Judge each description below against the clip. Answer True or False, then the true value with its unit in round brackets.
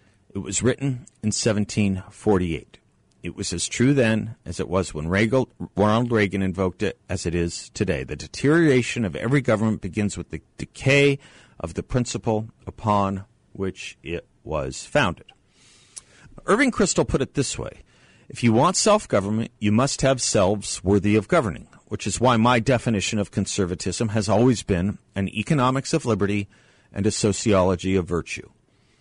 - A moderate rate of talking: True (155 wpm)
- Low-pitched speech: True (105 Hz)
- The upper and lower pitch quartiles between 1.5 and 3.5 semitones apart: False (4.2 semitones)